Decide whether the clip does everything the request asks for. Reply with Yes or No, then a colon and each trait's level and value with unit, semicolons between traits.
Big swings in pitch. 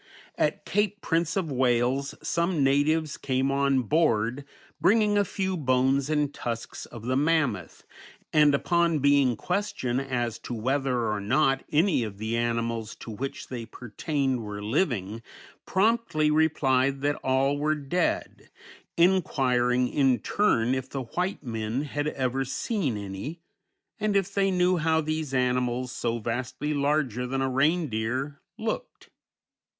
No: average, 4.3 semitones